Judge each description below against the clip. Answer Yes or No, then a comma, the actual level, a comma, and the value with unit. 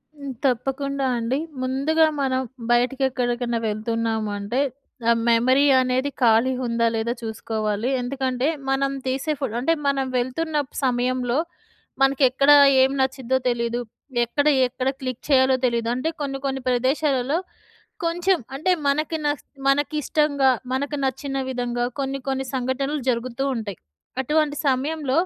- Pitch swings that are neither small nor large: No, narrow, 2.3 semitones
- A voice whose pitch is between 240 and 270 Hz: Yes, very high, 260 Hz